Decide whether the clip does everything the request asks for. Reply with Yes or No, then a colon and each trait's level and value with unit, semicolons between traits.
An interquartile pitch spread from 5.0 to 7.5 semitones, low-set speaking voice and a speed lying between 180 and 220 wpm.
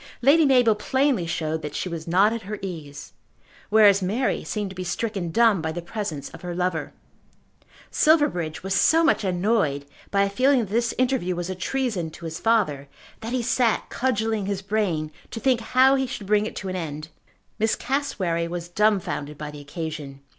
No: wide, 5.6 semitones; high, 195 Hz; average, 190 wpm